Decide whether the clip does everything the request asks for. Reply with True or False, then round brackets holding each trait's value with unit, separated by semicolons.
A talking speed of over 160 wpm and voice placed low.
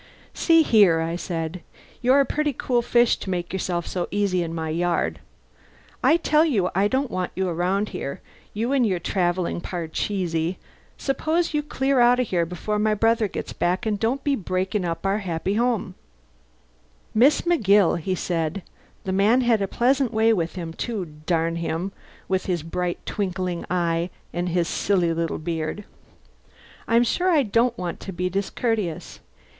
False (170 wpm; 190 Hz)